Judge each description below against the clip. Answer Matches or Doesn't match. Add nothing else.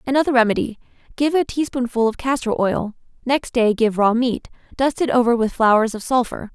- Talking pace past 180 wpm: Doesn't match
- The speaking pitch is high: Matches